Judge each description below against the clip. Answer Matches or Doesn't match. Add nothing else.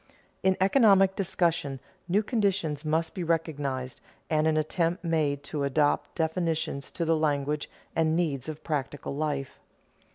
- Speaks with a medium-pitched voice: Matches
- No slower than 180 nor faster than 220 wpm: Doesn't match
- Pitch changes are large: Doesn't match